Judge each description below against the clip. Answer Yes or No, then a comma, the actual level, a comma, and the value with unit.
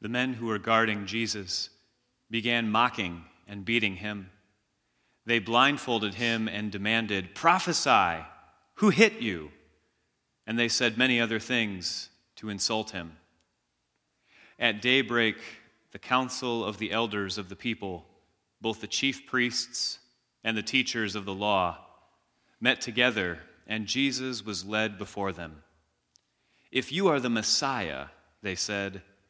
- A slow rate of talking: Yes, slow, 130 wpm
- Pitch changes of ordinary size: Yes, average, 3.3 semitones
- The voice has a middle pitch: No, low, 110 Hz